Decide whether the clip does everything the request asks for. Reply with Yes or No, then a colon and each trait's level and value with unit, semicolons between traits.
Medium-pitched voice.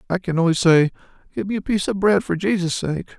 Yes: medium, 180 Hz